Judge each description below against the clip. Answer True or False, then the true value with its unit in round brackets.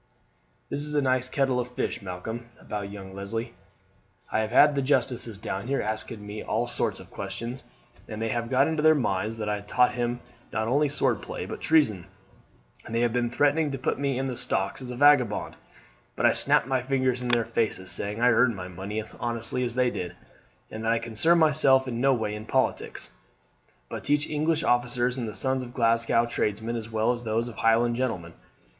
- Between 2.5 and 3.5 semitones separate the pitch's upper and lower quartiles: True (3.2 semitones)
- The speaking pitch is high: False (120 Hz)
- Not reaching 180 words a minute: False (205 wpm)